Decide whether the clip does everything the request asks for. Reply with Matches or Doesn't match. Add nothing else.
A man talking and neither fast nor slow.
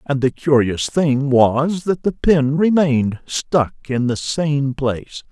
Matches